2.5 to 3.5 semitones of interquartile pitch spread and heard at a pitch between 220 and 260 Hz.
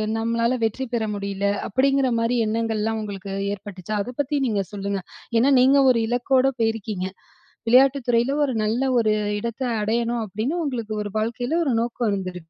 Yes: average, 3.1 semitones; high, 230 Hz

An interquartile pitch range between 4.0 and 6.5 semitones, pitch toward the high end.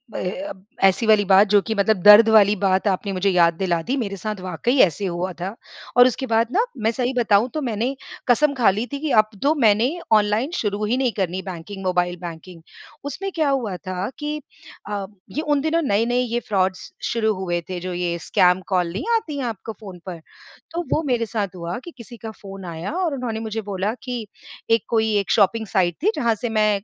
Yes: average, 4.4 semitones; high, 215 Hz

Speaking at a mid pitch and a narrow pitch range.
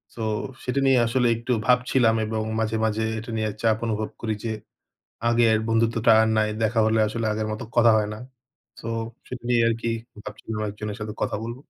No: low, 115 Hz; narrow, 1.4 semitones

